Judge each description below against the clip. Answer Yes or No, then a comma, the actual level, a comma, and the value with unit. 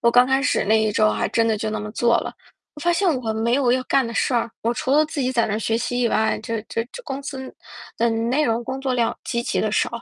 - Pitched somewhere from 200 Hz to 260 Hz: Yes, high, 235 Hz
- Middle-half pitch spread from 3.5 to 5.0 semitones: No, average, 2.8 semitones